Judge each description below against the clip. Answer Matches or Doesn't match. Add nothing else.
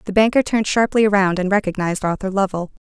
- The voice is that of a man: Doesn't match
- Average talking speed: Matches